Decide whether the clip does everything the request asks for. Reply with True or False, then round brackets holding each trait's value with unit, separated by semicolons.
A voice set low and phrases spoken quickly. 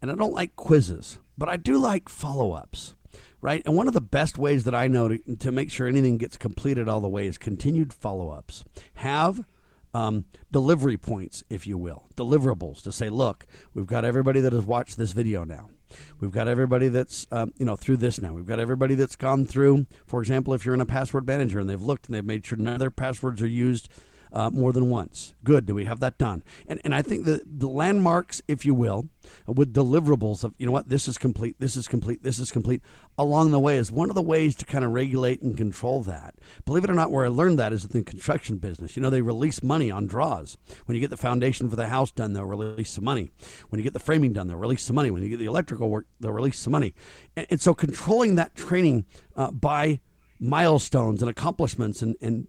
True (125 Hz; 235 wpm)